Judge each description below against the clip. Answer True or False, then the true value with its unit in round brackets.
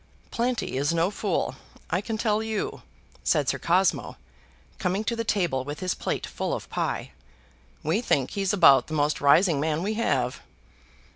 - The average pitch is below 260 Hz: True (185 Hz)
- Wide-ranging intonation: True (6.2 semitones)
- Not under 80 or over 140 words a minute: False (165 wpm)